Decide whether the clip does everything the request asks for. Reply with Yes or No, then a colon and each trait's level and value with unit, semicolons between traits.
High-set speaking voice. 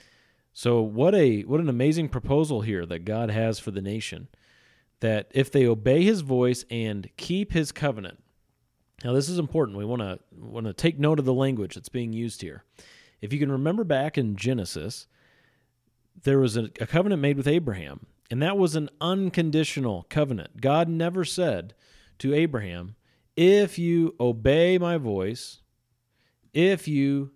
No: low, 130 Hz